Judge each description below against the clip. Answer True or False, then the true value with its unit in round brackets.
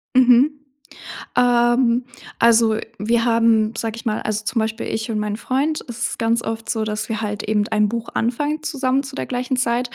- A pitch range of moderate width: False (2.3 semitones)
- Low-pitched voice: False (230 Hz)